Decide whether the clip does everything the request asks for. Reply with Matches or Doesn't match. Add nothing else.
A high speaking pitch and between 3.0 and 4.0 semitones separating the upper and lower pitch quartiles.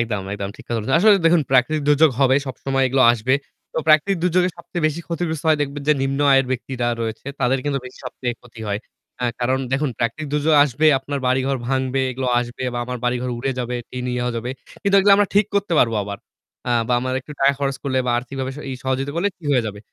Doesn't match